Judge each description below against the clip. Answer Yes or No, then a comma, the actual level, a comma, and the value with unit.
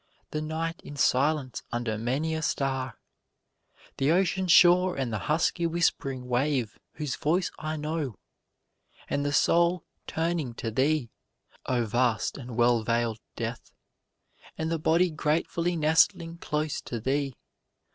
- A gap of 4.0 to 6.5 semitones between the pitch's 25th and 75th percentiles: Yes, average, 4.7 semitones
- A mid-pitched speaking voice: Yes, medium, 150 Hz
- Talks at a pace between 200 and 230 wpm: No, slow, 135 wpm